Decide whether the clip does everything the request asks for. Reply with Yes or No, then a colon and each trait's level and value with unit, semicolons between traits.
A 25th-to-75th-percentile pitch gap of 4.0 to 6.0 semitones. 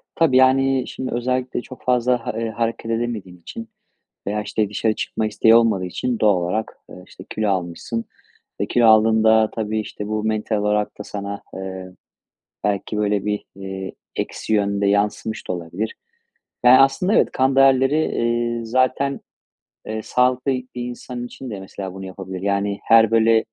No: average, 3.4 semitones